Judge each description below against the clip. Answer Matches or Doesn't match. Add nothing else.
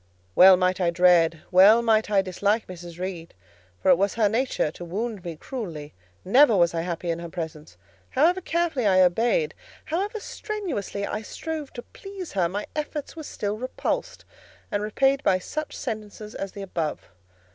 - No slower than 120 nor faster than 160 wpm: Doesn't match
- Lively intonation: Matches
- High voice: Matches